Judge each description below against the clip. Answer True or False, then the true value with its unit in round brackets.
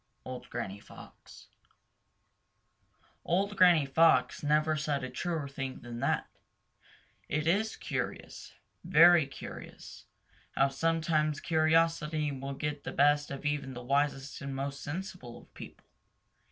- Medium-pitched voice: True (150 Hz)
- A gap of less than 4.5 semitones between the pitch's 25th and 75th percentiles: True (3.1 semitones)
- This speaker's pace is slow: True (125 wpm)